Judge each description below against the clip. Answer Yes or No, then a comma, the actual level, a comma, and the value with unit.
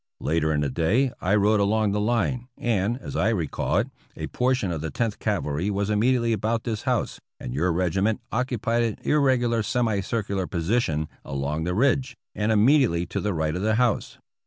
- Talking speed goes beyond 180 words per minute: Yes, average, 190 wpm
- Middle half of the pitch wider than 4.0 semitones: Yes, average, 5.0 semitones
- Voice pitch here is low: Yes, low, 105 Hz